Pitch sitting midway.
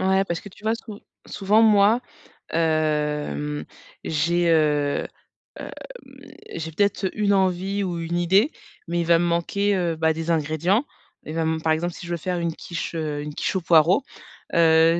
Yes: medium, 170 Hz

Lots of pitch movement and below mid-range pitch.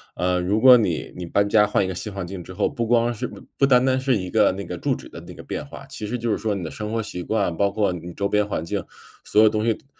No: average, 3.6 semitones; low, 105 Hz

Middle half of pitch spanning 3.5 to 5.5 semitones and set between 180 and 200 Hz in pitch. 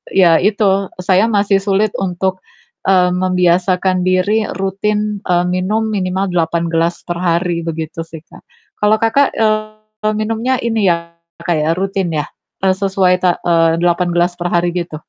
No: average, 3.1 semitones; medium, 185 Hz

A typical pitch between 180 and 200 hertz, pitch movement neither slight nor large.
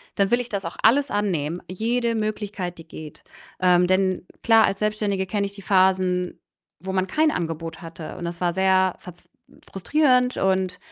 Yes: high, 190 Hz; average, 3.0 semitones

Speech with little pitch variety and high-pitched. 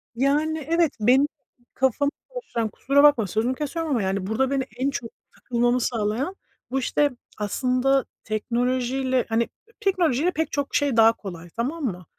No: average, 3.9 semitones; very high, 255 Hz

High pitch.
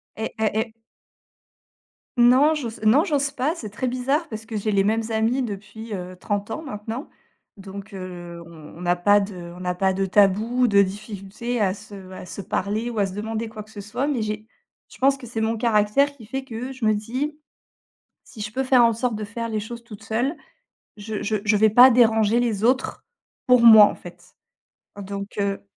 Yes: high, 220 Hz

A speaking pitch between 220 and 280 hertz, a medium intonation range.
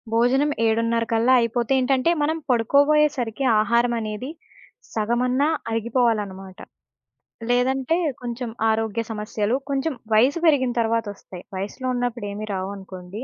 Yes: high, 235 Hz; average, 3.1 semitones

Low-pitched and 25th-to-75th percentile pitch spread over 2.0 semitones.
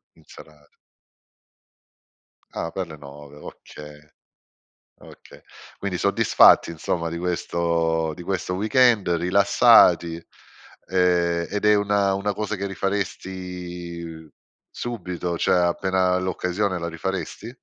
Yes: very low, 90 Hz; average, 2.7 semitones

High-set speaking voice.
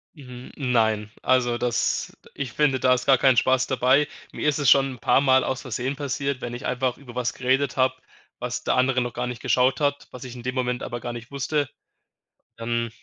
No: low, 130 Hz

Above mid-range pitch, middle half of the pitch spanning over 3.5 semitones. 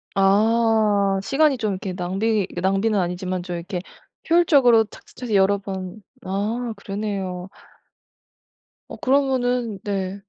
No: high, 200 Hz; average, 3.2 semitones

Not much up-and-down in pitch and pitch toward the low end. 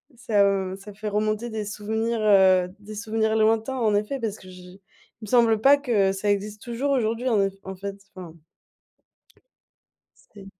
No: narrow, 2.3 semitones; high, 210 Hz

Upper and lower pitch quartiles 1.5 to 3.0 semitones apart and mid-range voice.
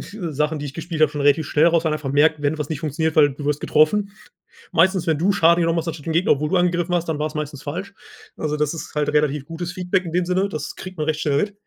Yes: average, 2.7 semitones; medium, 160 Hz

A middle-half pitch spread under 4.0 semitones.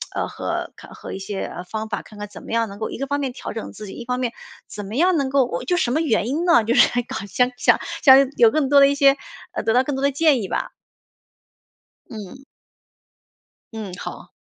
No: average, 4.3 semitones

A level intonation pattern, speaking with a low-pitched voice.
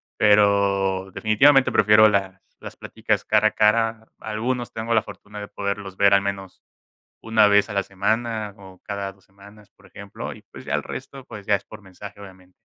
Yes: narrow, 1.7 semitones; low, 100 Hz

